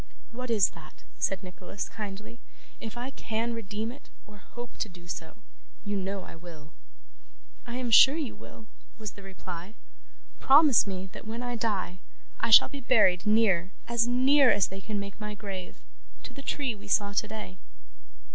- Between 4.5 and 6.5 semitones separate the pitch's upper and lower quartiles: No, average, 3.7 semitones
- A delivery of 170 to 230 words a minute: Yes, average, 175 wpm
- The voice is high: Yes, high, 210 Hz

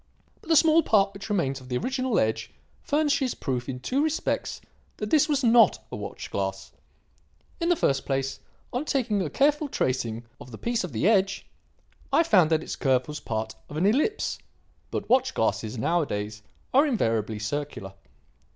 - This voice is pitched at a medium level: Yes, medium, 180 Hz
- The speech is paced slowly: No, average, 175 wpm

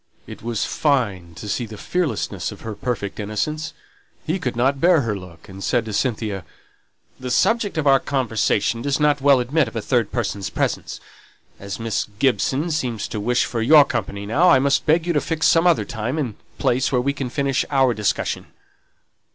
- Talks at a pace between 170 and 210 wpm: Yes, average, 190 wpm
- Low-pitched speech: Yes, low, 125 Hz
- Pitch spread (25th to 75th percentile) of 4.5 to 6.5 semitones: Yes, average, 4.8 semitones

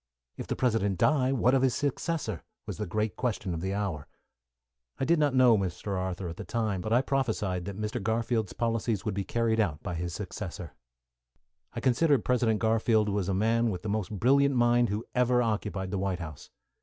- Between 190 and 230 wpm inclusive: Yes, average, 200 wpm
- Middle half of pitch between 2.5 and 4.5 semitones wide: Yes, average, 4.1 semitones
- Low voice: Yes, low, 110 Hz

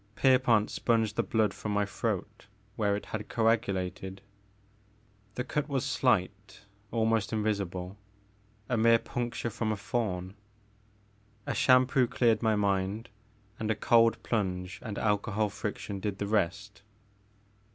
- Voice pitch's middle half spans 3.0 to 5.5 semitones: No, narrow, 2.5 semitones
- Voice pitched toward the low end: Yes, low, 105 Hz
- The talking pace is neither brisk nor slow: No, slow, 130 wpm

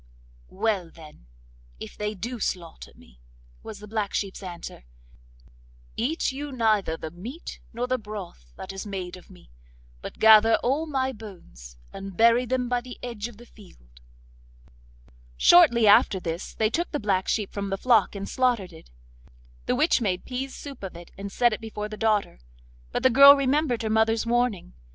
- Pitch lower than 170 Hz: No, high, 215 Hz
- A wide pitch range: No, average, 4.5 semitones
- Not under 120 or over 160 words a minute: No, average, 175 wpm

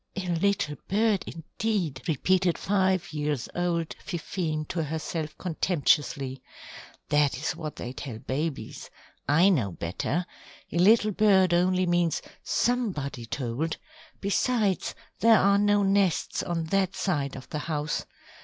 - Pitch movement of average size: Yes, average, 4.6 semitones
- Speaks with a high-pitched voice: No, medium, 170 Hz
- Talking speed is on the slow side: Yes, slow, 125 wpm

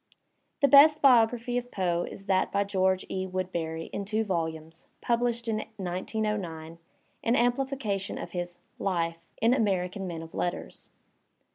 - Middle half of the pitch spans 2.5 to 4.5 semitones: No, average, 4.9 semitones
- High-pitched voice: Yes, high, 195 Hz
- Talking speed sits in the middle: Yes, average, 145 wpm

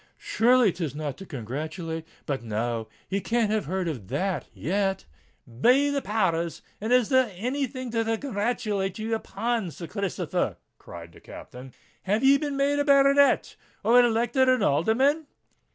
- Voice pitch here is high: Yes, high, 215 Hz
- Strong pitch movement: Yes, wide, 7.7 semitones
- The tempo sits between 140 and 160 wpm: Yes, average, 150 wpm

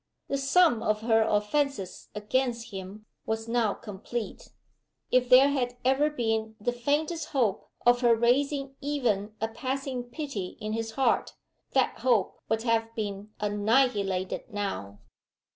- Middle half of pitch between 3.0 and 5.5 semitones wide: Yes, average, 3.9 semitones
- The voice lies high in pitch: Yes, high, 230 Hz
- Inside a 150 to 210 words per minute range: No, slow, 135 wpm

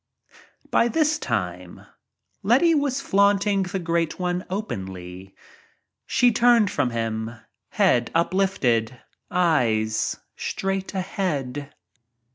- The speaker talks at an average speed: No, slow, 90 wpm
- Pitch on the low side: No, medium, 175 Hz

